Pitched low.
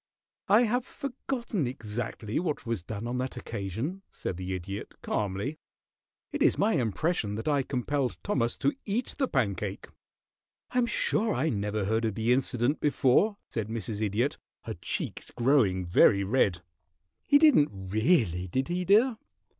Yes: low, 120 Hz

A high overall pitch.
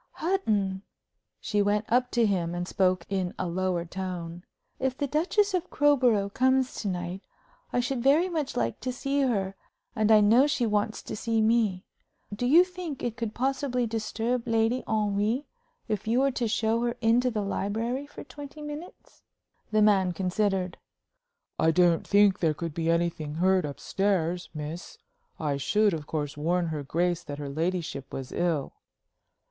Yes: high, 210 Hz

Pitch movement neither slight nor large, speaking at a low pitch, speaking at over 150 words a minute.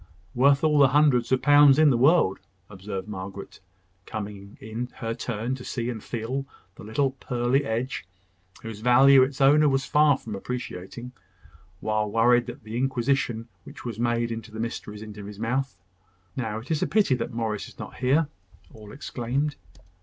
Yes: average, 3.6 semitones; low, 120 Hz; average, 170 wpm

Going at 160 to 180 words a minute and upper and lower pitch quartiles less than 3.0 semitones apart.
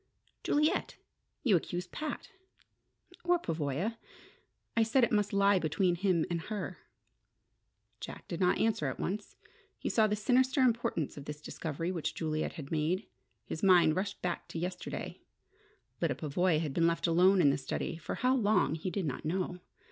No: average, 170 wpm; average, 4.6 semitones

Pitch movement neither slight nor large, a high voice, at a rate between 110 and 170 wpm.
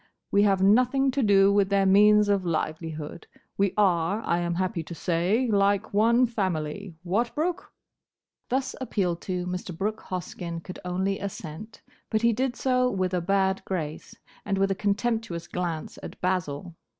Yes: average, 3.5 semitones; high, 195 Hz; average, 160 wpm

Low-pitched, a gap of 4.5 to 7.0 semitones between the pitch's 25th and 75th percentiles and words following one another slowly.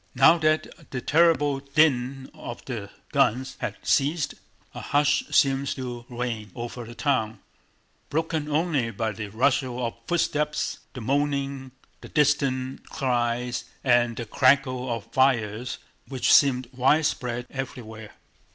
No: low, 130 Hz; average, 3.0 semitones; slow, 125 wpm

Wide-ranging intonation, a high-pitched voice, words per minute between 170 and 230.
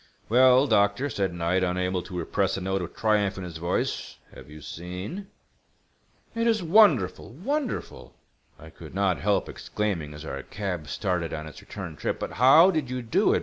No: wide, 6.5 semitones; very low, 95 Hz; average, 175 wpm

